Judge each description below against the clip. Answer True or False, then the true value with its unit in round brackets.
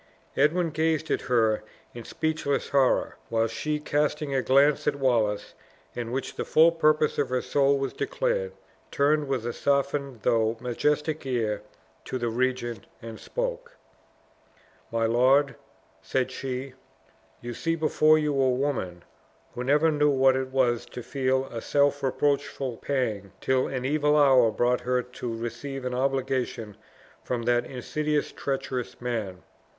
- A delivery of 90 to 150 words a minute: True (145 wpm)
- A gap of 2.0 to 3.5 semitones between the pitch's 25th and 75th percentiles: True (3.2 semitones)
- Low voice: True (130 Hz)